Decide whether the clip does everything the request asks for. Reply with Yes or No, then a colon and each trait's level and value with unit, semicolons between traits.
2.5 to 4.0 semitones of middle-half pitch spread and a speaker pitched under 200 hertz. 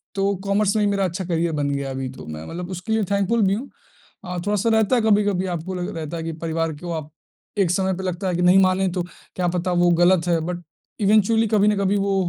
Yes: average, 2.9 semitones; medium, 185 Hz